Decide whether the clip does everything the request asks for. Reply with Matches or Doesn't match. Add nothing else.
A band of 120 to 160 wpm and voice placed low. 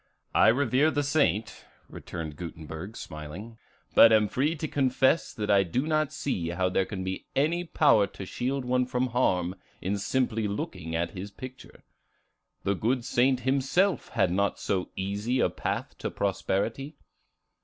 Matches